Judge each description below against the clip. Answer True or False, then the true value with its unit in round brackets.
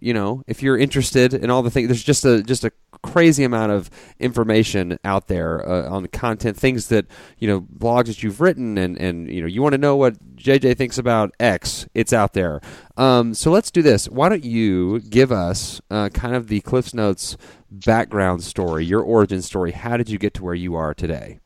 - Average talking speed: False (220 wpm)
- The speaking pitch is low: True (110 Hz)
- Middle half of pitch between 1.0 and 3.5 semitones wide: False (4.8 semitones)